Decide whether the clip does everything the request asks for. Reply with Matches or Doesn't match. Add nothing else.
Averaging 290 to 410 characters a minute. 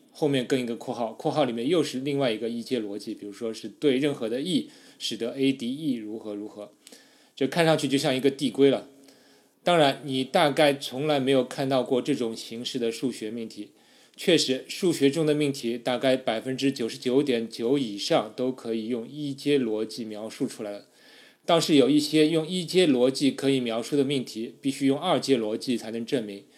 Matches